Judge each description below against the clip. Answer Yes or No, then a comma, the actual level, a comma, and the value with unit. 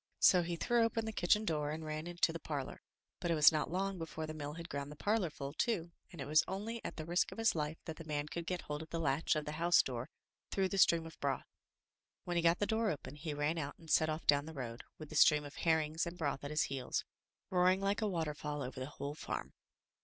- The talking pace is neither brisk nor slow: No, fast, 255 wpm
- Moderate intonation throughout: Yes, average, 3.0 semitones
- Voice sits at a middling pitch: Yes, medium, 160 Hz